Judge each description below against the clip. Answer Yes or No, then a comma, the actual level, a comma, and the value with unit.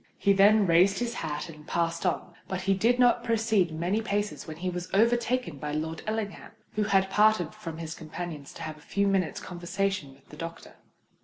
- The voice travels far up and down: No, average, 4.2 semitones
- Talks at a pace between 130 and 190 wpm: No, average, 200 wpm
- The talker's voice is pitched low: No, medium, 185 Hz